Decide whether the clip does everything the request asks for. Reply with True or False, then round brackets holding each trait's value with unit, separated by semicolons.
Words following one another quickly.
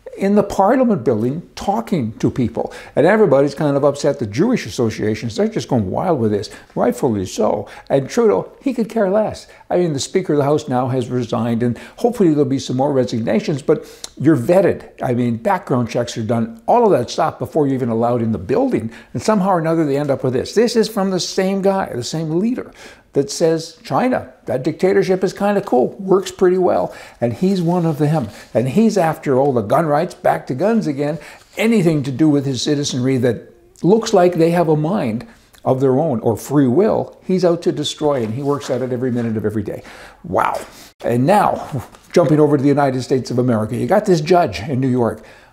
True (215 wpm)